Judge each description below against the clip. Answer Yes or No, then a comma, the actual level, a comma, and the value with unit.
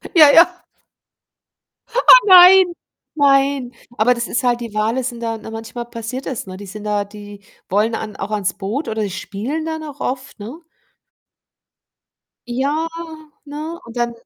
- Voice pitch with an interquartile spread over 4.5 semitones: Yes, average, 5.0 semitones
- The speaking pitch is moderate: No, high, 240 Hz